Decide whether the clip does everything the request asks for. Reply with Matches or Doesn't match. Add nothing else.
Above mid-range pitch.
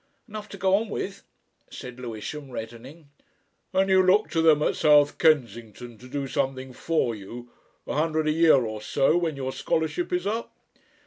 Doesn't match